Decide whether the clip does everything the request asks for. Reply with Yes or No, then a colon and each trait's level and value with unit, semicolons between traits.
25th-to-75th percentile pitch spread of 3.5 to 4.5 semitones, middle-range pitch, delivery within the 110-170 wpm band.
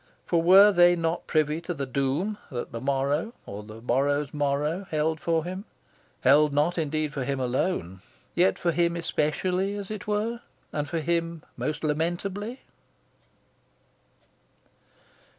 Yes: average, 3.8 semitones; medium, 160 Hz; average, 140 wpm